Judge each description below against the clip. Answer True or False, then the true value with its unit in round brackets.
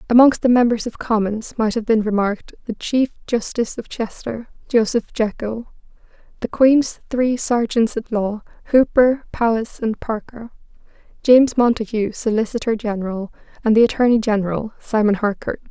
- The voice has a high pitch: True (225 Hz)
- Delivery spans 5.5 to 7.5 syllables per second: False (5.0 syllables/s)